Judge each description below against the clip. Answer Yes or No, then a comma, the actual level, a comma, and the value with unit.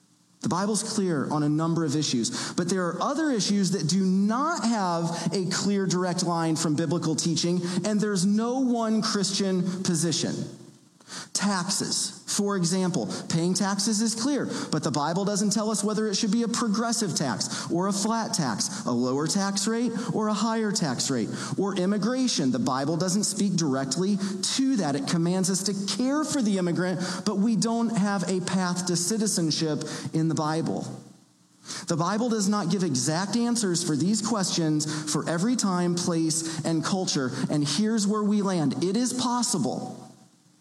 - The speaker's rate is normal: Yes, average, 170 wpm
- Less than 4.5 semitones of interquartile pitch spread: Yes, average, 4.1 semitones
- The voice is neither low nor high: No, high, 195 Hz